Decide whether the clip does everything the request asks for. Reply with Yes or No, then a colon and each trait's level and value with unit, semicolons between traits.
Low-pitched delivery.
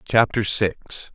Yes: low, 105 Hz